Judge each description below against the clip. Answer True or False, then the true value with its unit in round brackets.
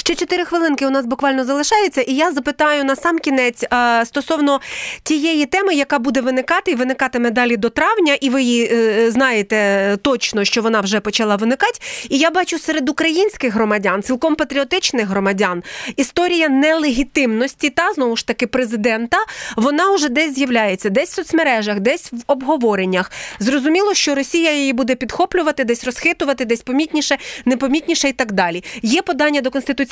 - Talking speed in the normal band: False (160 wpm)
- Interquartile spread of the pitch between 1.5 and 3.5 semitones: False (4.9 semitones)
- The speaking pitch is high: True (275 Hz)